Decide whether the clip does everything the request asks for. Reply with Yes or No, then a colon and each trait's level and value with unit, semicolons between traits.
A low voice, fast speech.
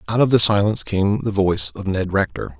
Yes: low, 100 Hz; fast, 230 wpm